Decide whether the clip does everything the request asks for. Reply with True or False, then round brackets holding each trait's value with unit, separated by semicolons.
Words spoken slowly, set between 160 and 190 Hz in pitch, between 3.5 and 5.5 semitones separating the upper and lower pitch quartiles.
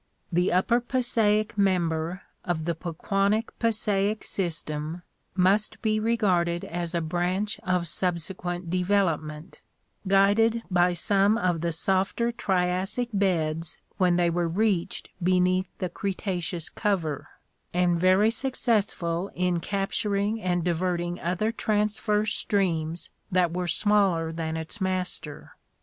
False (120 wpm; 185 Hz; 3.1 semitones)